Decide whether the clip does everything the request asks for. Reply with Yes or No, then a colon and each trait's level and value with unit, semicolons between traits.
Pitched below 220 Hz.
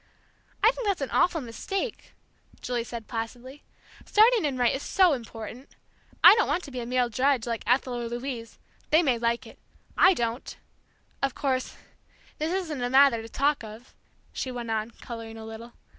No: very high, 250 Hz